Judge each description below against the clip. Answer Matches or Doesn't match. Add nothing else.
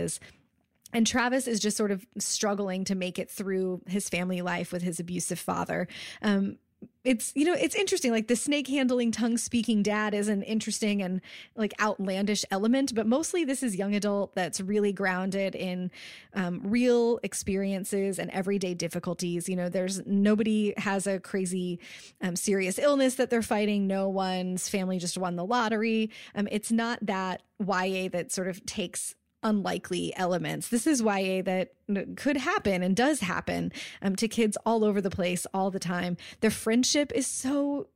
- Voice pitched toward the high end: Matches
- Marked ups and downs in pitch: Doesn't match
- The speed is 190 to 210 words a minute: Doesn't match